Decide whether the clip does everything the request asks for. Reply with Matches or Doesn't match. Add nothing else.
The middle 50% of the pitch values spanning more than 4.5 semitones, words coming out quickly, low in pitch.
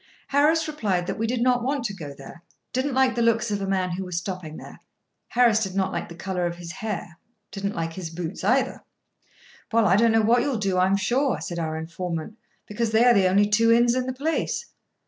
Doesn't match